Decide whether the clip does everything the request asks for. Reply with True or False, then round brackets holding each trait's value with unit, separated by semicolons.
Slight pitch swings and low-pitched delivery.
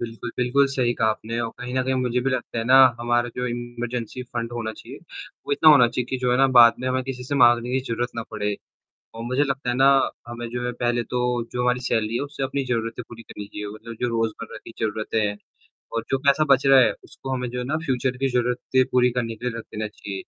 True (1.8 semitones; 120 Hz)